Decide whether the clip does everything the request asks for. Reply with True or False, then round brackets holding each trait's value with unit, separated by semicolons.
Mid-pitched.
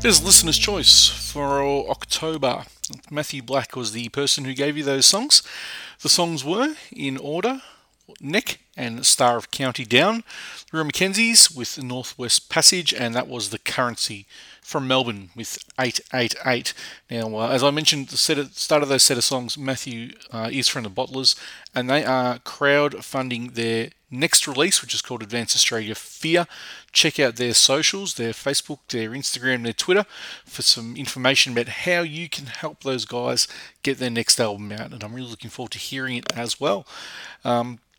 False (130 Hz)